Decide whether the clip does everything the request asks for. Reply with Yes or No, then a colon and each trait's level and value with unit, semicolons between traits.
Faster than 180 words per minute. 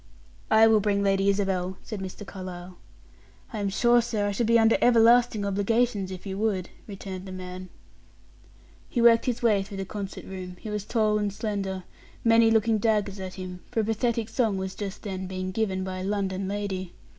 Yes: average, 190 wpm